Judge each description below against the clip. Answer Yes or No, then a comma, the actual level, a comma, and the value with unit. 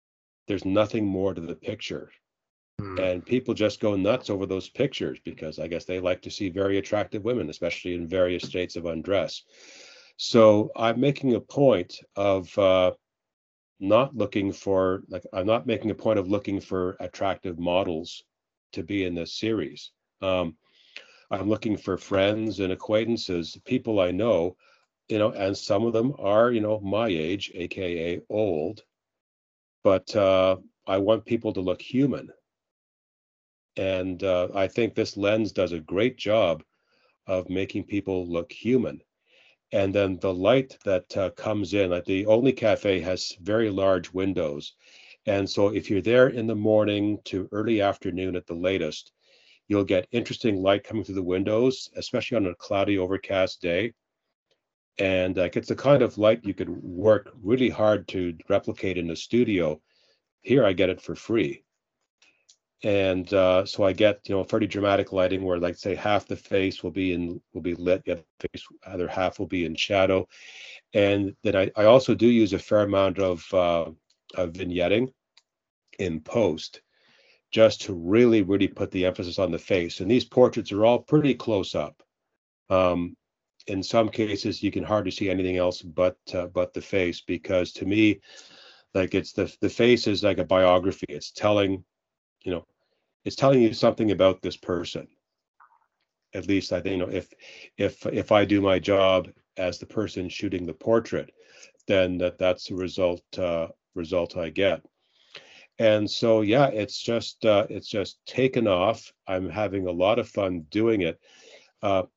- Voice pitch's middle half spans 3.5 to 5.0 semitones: No, average, 2.9 semitones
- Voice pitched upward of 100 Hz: No, very low, 95 Hz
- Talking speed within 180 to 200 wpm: No, average, 170 wpm